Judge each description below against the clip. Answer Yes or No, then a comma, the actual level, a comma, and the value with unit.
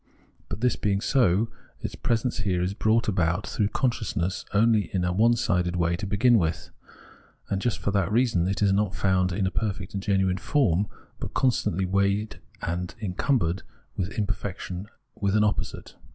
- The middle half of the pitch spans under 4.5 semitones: Yes, average, 3.0 semitones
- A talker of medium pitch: No, low, 100 Hz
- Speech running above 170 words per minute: No, average, 165 wpm